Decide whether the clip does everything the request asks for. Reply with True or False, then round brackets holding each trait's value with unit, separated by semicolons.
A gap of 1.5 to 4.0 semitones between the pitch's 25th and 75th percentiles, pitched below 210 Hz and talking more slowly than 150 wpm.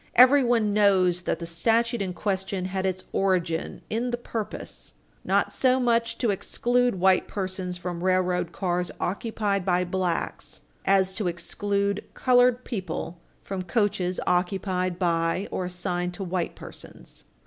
True (3.2 semitones; 190 Hz; 135 wpm)